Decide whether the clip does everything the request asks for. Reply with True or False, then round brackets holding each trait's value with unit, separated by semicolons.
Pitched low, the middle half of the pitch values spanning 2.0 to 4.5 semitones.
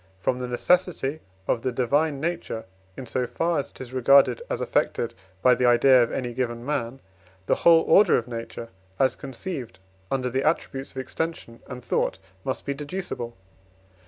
True (130 Hz; 3.5 semitones)